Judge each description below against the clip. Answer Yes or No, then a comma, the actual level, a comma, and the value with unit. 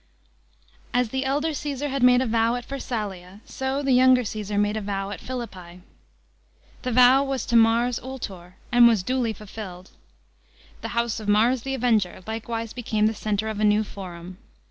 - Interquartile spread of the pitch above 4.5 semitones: No, average, 3.4 semitones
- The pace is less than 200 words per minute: Yes, average, 175 wpm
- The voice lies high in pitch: Yes, high, 225 Hz